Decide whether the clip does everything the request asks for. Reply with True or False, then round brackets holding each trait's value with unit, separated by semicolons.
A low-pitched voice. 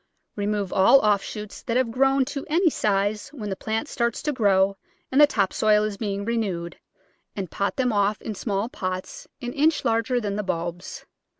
False (215 Hz)